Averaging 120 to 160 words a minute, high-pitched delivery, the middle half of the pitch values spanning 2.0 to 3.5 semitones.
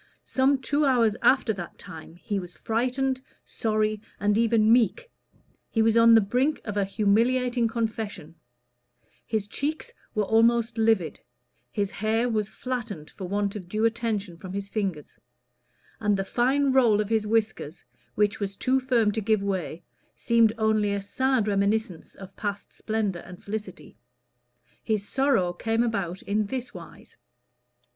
Yes: average, 150 wpm; high, 220 Hz; average, 2.7 semitones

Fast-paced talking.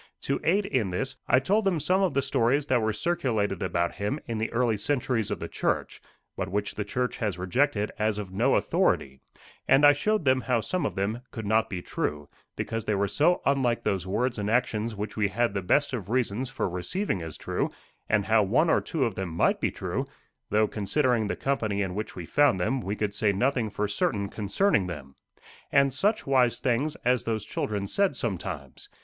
Yes: fast, 210 wpm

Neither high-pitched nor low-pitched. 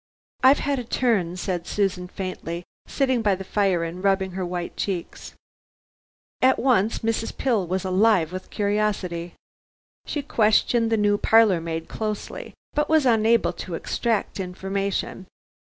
No: high, 200 Hz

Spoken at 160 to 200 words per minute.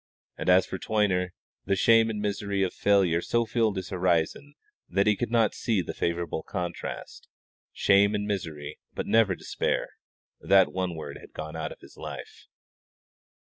Yes: average, 165 wpm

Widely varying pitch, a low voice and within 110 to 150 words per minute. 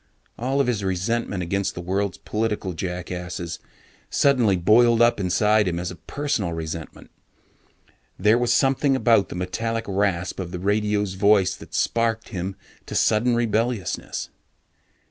No: average, 4.2 semitones; low, 100 Hz; average, 140 wpm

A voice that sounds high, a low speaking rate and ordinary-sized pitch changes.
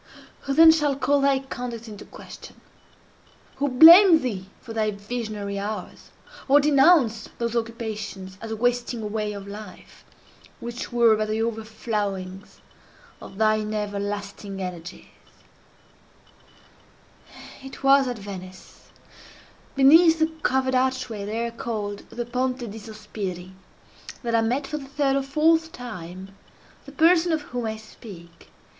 Yes: high, 230 Hz; slow, 130 wpm; average, 4.5 semitones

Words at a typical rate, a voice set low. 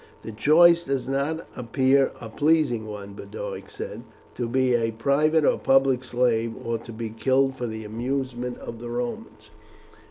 Yes: average, 160 wpm; low, 125 Hz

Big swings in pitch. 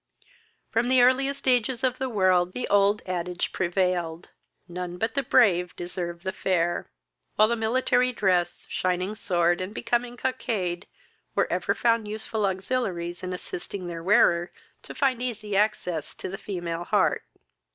No: average, 5.0 semitones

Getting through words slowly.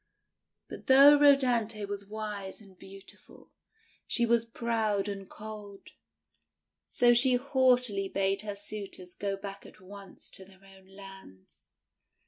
Yes: slow, 125 wpm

